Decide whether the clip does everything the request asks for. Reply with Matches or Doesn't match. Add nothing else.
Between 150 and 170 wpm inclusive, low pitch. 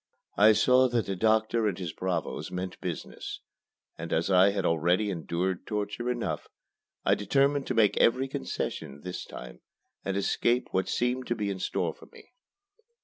Matches